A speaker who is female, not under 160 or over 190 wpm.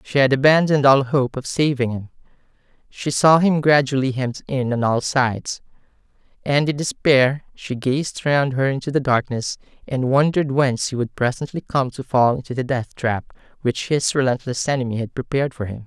No: male; average, 180 wpm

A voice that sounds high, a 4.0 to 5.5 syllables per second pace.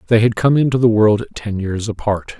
No: low, 110 Hz; 5.2 syllables/s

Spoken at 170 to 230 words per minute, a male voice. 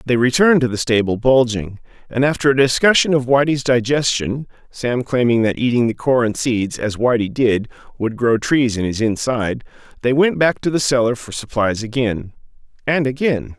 Yes: average, 175 wpm; male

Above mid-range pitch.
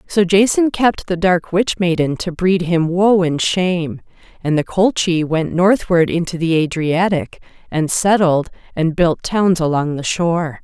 No: medium, 175 Hz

